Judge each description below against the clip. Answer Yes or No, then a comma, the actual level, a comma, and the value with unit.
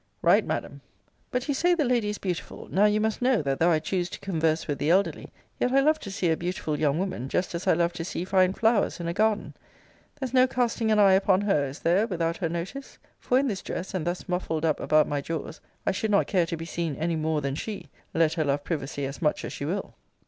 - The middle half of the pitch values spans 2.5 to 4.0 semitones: No, average, 4.7 semitones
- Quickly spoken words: Yes, fast, 250 wpm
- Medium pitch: Yes, medium, 180 Hz